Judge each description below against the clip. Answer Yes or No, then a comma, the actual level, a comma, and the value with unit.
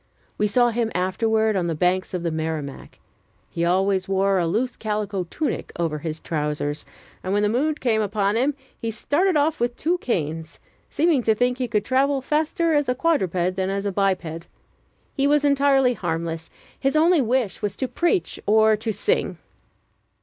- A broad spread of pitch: Yes, wide, 6.7 semitones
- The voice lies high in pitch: Yes, high, 215 Hz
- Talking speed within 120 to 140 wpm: No, average, 180 wpm